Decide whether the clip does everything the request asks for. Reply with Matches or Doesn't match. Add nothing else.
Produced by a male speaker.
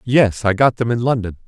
Matches